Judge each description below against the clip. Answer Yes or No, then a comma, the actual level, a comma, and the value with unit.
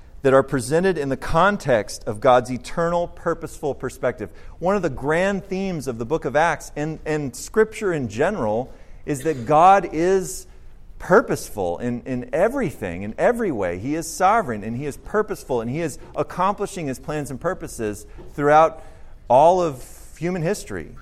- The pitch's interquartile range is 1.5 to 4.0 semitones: No, wide, 5.6 semitones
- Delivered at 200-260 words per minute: No, average, 165 wpm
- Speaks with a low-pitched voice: No, medium, 155 Hz